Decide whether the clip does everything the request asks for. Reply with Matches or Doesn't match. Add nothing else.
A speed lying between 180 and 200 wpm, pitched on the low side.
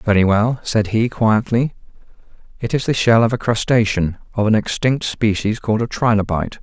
Doesn't match